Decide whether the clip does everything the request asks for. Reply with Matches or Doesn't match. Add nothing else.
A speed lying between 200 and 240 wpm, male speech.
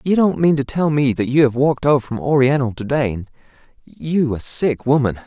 Matches